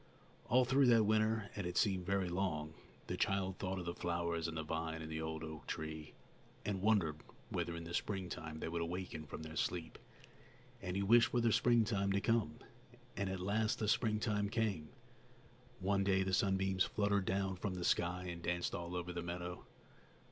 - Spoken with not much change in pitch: No, average, 3.2 semitones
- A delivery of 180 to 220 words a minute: Yes, average, 190 wpm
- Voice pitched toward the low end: Yes, very low, 95 Hz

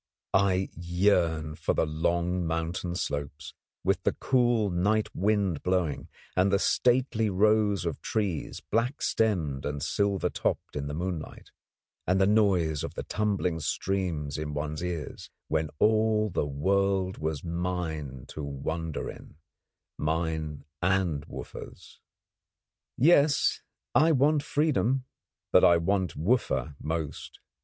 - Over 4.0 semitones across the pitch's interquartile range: Yes, average, 4.8 semitones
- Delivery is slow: Yes, slow, 125 wpm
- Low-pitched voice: Yes, very low, 90 Hz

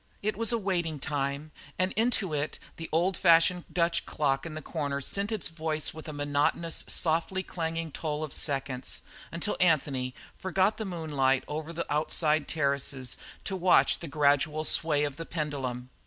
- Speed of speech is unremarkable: Yes, average, 165 wpm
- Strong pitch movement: No, average, 3.1 semitones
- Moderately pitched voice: Yes, medium, 155 Hz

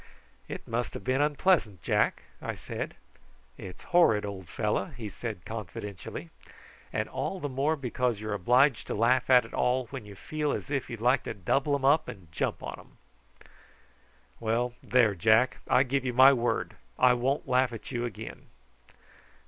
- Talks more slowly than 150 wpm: No, average, 175 wpm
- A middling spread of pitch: Yes, average, 3.9 semitones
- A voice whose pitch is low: Yes, low, 125 Hz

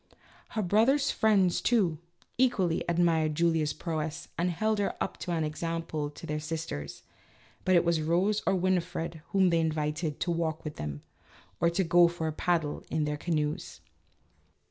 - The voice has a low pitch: No, medium, 170 Hz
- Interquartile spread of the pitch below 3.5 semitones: Yes, narrow, 2.6 semitones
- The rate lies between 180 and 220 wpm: No, average, 165 wpm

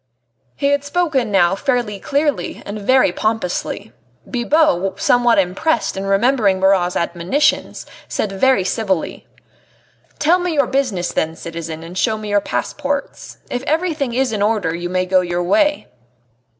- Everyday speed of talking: Yes, average, 145 wpm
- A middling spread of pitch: No, wide, 7.1 semitones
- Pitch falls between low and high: No, high, 215 Hz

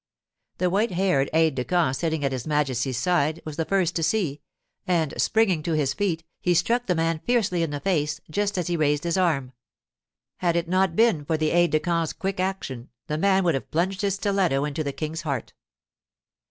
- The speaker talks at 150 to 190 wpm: No, fast, 205 wpm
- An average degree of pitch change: Yes, average, 3.9 semitones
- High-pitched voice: No, medium, 165 Hz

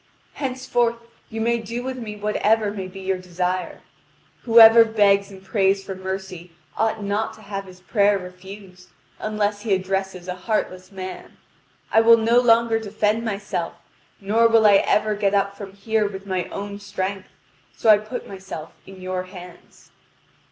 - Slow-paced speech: No, average, 160 wpm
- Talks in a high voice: Yes, high, 200 Hz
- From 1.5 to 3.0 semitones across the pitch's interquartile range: Yes, average, 2.7 semitones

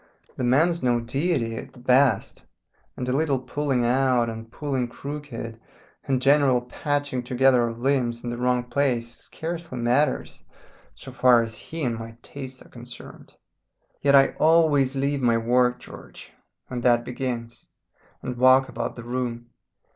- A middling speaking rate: Yes, average, 155 wpm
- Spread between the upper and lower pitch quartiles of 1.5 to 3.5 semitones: Yes, narrow, 2.6 semitones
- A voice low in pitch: Yes, low, 125 Hz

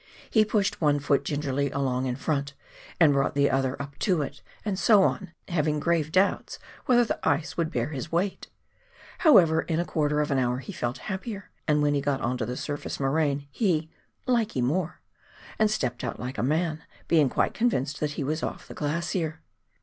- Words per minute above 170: Yes, average, 200 wpm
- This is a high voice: No, medium, 150 Hz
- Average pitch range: Yes, average, 3.8 semitones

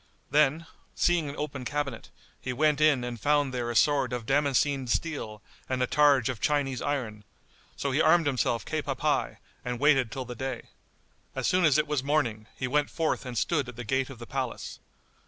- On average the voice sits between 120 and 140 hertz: Yes, low, 135 Hz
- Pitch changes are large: No, average, 3.1 semitones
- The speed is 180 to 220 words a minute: Yes, average, 200 wpm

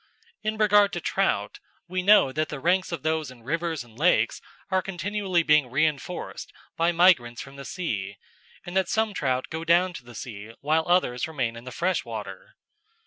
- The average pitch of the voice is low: No, medium, 160 Hz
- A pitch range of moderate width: No, wide, 5.9 semitones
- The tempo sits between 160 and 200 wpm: Yes, average, 180 wpm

